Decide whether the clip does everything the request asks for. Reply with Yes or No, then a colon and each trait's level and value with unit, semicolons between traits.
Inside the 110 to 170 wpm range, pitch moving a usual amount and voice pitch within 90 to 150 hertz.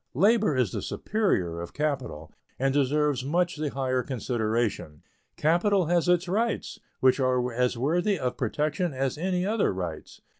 No: average, 150 wpm; wide, 5.9 semitones; medium, 140 Hz